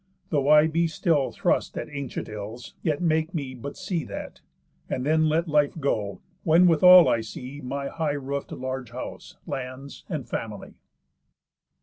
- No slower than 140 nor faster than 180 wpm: Yes, average, 160 wpm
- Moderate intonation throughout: Yes, average, 3.6 semitones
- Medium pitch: Yes, medium, 145 Hz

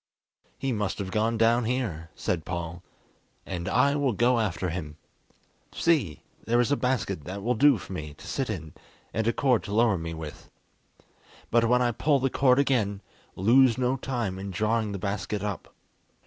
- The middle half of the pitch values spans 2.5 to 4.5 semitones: No, average, 5.0 semitones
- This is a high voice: No, low, 110 Hz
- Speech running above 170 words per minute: Yes, average, 180 wpm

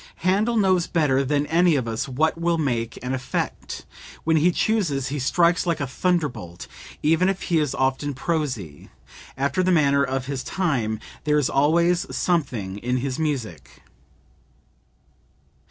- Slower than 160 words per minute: Yes, average, 150 wpm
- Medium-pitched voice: Yes, medium, 145 Hz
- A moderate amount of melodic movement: Yes, average, 4.8 semitones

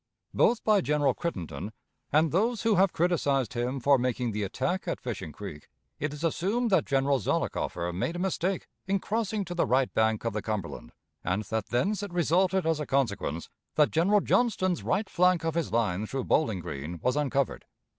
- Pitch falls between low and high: Yes, medium, 145 Hz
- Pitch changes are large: Yes, wide, 8.4 semitones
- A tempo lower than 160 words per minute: No, average, 185 wpm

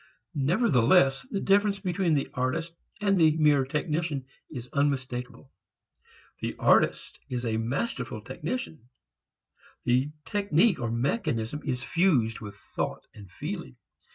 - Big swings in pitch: Yes, wide, 6.1 semitones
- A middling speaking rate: No, slow, 120 wpm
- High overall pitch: No, medium, 140 Hz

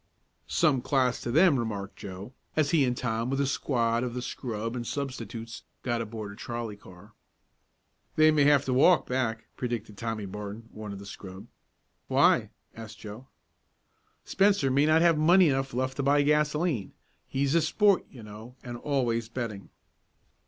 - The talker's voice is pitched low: Yes, low, 125 Hz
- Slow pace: No, average, 165 wpm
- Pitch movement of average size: Yes, average, 4.2 semitones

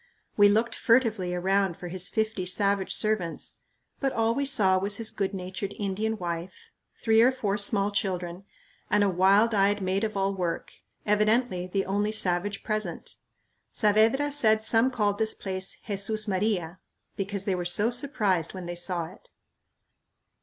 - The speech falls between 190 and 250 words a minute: No, average, 160 wpm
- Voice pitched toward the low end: No, high, 200 Hz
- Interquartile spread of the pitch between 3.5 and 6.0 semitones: No, average, 2.8 semitones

